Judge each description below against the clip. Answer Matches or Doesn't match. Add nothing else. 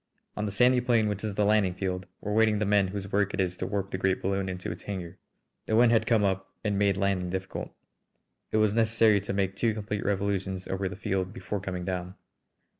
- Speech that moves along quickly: Matches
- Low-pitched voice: Matches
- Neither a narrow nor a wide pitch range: Doesn't match